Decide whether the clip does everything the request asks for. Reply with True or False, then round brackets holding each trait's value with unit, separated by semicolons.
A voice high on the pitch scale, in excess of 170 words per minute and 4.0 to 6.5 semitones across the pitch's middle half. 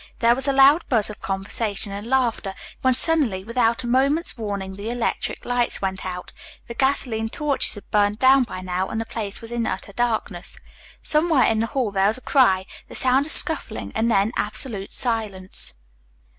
True (225 Hz; 185 wpm; 4.4 semitones)